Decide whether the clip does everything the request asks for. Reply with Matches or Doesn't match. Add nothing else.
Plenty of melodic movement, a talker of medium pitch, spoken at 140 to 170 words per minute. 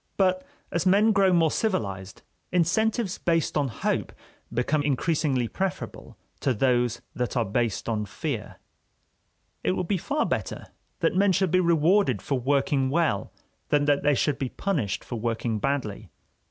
Matches